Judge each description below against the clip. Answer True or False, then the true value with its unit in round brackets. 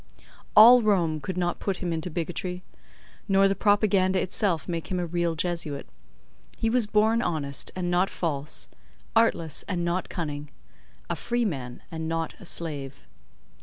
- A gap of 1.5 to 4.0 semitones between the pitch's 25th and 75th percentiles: True (3.7 semitones)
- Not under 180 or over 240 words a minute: False (145 wpm)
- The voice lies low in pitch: False (175 Hz)